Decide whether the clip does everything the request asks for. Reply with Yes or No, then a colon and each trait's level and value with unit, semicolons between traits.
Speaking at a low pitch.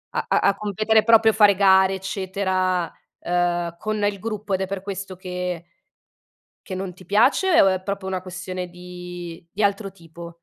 No: high, 190 Hz